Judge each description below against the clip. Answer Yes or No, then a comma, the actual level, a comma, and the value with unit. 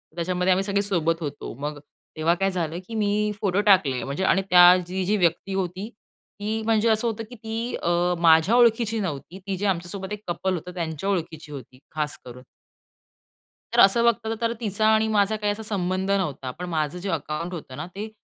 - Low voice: No, medium, 185 Hz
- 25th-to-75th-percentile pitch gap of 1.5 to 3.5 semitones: No, average, 4.1 semitones